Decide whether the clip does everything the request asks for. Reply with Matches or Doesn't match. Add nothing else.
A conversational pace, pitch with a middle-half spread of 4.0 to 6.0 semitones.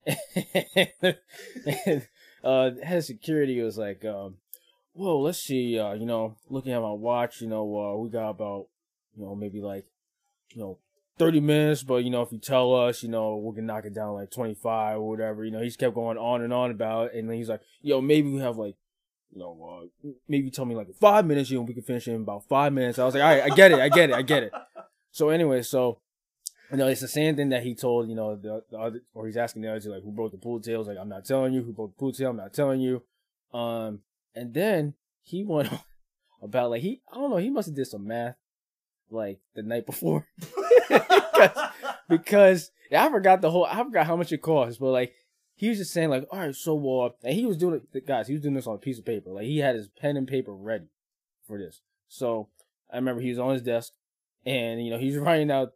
Doesn't match